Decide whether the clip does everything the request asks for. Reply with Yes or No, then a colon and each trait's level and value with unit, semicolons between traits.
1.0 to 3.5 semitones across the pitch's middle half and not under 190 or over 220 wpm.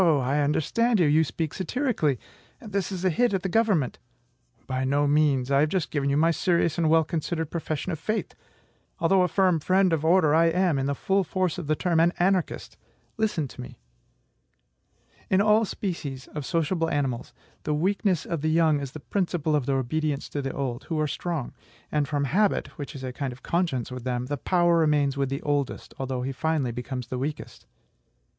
No: average, 4.2 semitones; average, 200 wpm